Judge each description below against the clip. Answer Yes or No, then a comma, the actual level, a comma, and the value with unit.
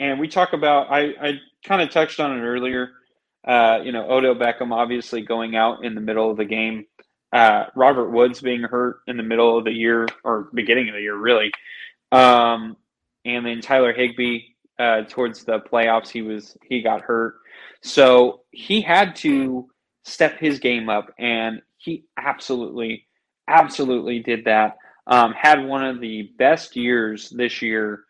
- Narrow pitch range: Yes, narrow, 2.2 semitones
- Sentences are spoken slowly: No, average, 170 wpm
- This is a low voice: Yes, low, 120 Hz